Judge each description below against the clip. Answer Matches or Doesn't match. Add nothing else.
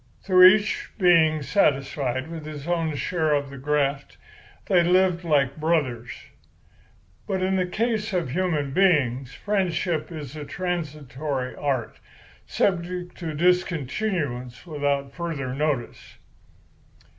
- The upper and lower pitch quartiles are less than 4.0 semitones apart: Doesn't match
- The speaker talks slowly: Matches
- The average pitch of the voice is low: Doesn't match